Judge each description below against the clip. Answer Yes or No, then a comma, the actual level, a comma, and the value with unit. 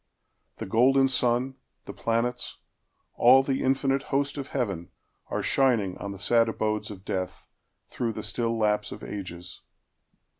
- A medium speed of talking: No, slow, 125 wpm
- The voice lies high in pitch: No, low, 115 Hz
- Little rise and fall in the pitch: No, average, 4.3 semitones